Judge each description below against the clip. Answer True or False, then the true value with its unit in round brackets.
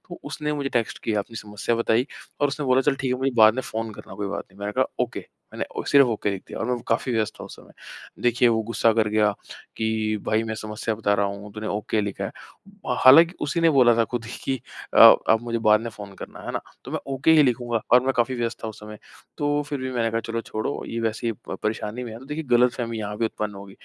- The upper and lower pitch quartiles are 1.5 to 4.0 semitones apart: True (2.9 semitones)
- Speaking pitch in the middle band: False (115 Hz)